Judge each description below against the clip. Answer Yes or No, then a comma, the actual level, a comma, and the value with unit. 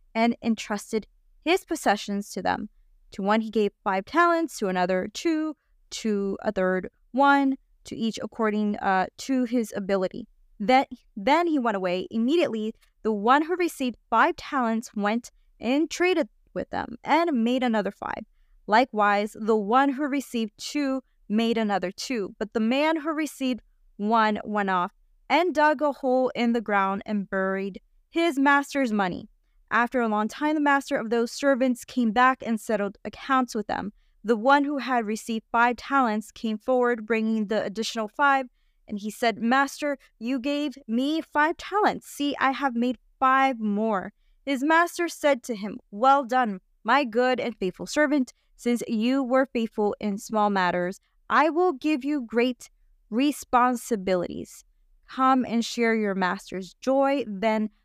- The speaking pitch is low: No, high, 240 Hz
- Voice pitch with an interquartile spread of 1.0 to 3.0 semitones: No, average, 4.5 semitones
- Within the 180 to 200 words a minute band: No, average, 160 wpm